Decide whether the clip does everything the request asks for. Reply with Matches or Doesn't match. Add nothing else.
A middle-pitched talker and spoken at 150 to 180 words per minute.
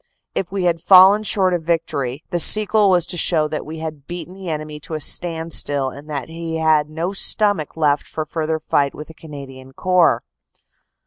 Doesn't match